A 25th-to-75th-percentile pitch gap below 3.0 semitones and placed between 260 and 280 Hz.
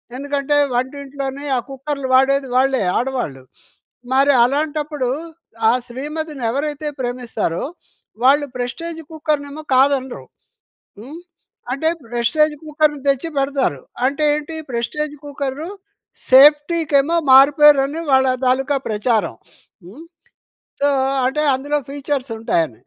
Yes: narrow, 2.4 semitones; very high, 275 Hz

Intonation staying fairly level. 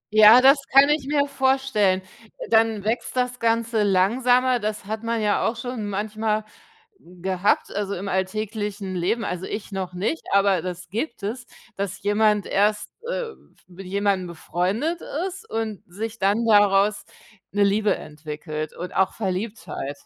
No: average, 3.3 semitones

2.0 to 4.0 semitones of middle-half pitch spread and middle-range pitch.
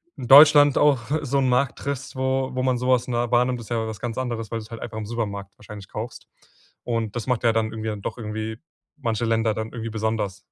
No: narrow, 2.5 semitones; low, 115 Hz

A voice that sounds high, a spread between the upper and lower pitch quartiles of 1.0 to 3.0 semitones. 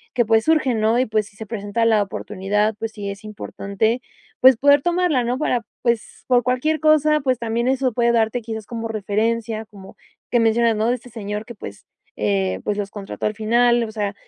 Yes: high, 225 Hz; average, 2.7 semitones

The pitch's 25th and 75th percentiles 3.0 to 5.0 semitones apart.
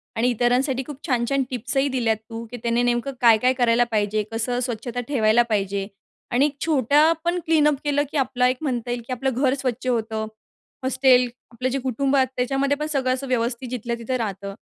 No: narrow, 2.5 semitones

